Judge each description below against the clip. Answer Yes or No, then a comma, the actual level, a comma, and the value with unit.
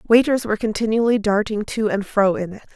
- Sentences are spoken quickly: No, average, 195 wpm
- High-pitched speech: Yes, high, 215 Hz